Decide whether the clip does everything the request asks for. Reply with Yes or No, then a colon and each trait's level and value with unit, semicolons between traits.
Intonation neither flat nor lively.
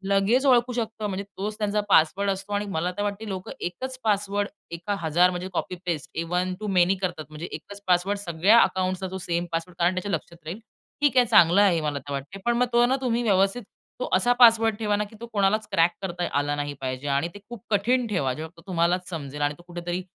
Yes: average, 3.6 semitones